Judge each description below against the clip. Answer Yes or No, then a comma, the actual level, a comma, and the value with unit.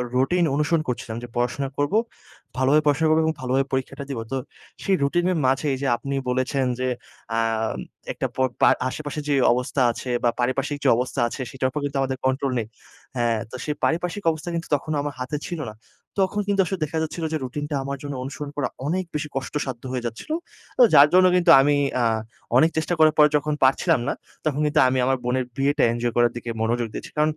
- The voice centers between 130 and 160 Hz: Yes, medium, 140 Hz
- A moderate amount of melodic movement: Yes, average, 3.2 semitones